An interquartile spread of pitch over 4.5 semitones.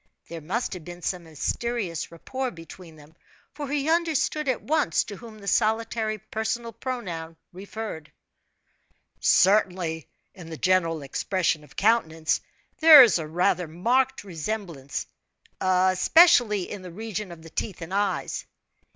Yes: wide, 5.6 semitones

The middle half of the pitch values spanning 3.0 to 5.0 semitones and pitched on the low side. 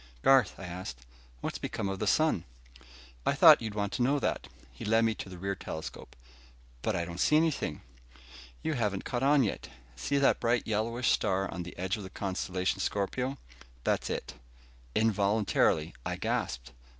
Yes: average, 4.7 semitones; low, 100 Hz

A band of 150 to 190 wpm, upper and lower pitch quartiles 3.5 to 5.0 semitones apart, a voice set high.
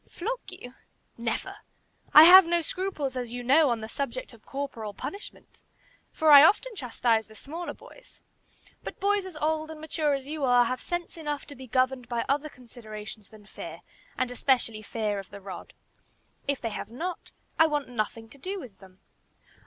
No: average, 185 wpm; wide, 5.6 semitones; very high, 270 Hz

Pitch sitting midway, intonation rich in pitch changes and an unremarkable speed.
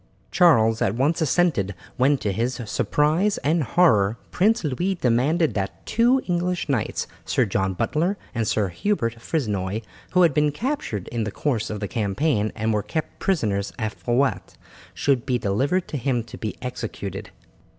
No: low, 125 Hz; wide, 7.2 semitones; average, 160 wpm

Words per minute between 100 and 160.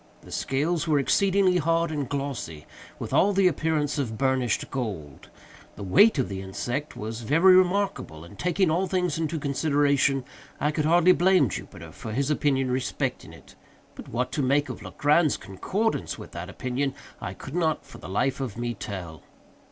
No: average, 175 wpm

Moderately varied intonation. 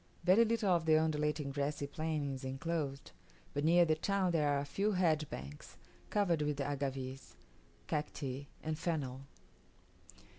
Yes: average, 3.2 semitones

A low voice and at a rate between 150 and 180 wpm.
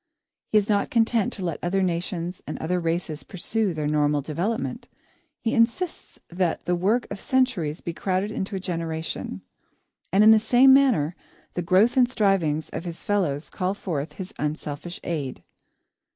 No: medium, 180 Hz; average, 165 wpm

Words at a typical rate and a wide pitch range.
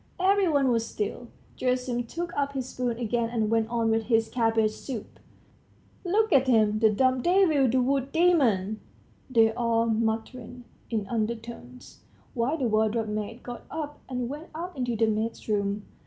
No: average, 165 wpm; average, 3.3 semitones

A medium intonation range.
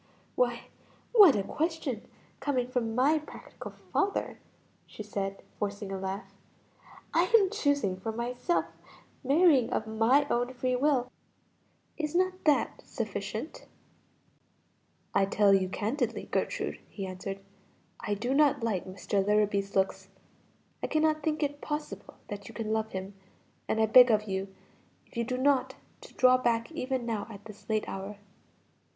No: wide, 5.9 semitones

